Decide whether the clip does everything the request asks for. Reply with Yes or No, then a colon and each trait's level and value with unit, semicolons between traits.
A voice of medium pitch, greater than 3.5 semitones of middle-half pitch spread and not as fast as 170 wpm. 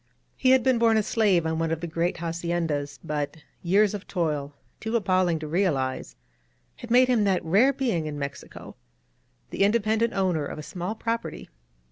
No: medium, 180 Hz; wide, 5.5 semitones; average, 175 wpm